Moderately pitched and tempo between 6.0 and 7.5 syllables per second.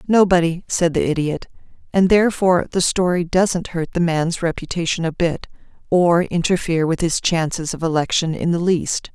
No: medium, 170 Hz; 5.1 syllables/s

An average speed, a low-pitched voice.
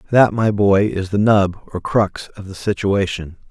Yes: average, 190 wpm; low, 100 Hz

